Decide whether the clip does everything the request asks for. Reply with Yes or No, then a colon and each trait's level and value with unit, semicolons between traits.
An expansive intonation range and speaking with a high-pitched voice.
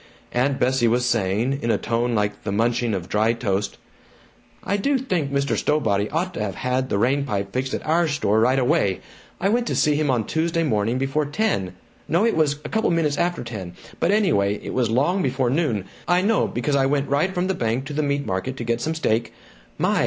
No: wide, 5.8 semitones; low, 135 Hz